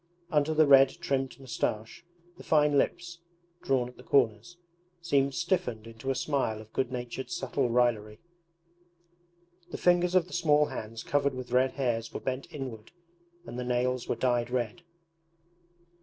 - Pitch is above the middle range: No, low, 130 Hz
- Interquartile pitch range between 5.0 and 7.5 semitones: No, average, 3.6 semitones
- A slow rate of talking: No, average, 155 wpm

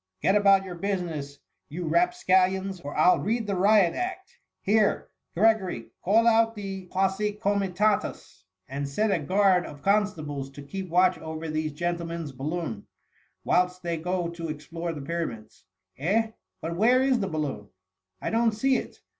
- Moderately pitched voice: Yes, medium, 180 Hz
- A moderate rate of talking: Yes, average, 165 wpm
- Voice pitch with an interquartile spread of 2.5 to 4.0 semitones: No, average, 4.7 semitones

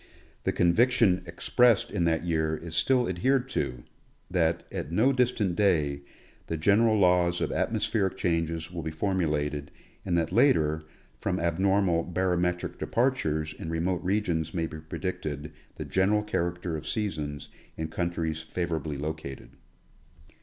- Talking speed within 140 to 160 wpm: Yes, average, 145 wpm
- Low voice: Yes, very low, 85 Hz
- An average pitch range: Yes, average, 3.5 semitones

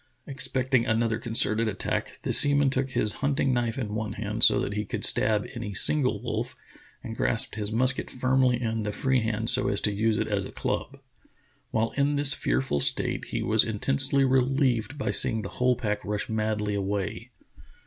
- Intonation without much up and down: No, average, 3.6 semitones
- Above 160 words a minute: Yes, average, 190 wpm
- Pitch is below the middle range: Yes, low, 115 Hz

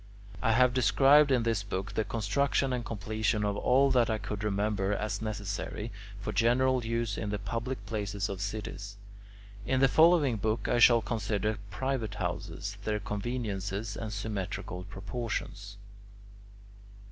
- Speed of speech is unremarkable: Yes, average, 145 wpm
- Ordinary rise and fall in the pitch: Yes, average, 3.0 semitones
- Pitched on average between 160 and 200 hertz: No, low, 110 Hz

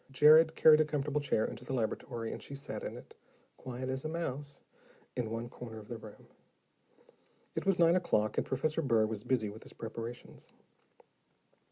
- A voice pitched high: No, low, 130 Hz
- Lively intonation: No, average, 4.8 semitones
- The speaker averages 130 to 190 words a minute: Yes, average, 180 wpm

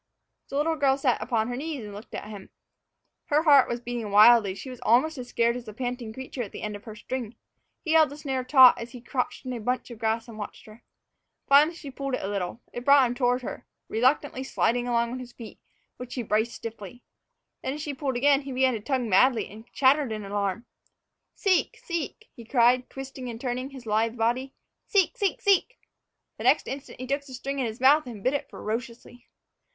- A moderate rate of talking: No, fast, 225 wpm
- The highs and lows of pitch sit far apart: No, average, 3.1 semitones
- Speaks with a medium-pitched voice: No, very high, 250 Hz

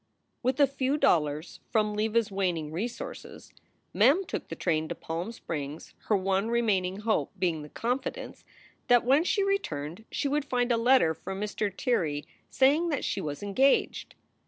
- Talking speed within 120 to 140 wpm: No, average, 165 wpm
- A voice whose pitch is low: No, high, 215 Hz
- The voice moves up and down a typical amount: No, wide, 7.1 semitones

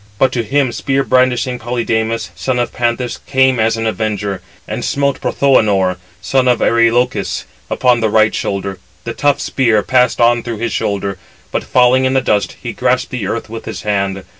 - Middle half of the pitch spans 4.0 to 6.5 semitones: No, average, 2.9 semitones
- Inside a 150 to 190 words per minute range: Yes, average, 180 wpm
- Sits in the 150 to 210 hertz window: No, low, 120 Hz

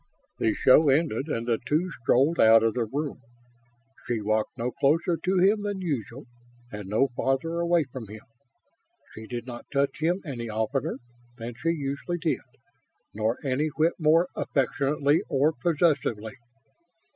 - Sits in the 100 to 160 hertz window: Yes, medium, 140 Hz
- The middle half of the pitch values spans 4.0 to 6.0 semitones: Yes, wide, 5.6 semitones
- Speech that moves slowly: No, average, 150 wpm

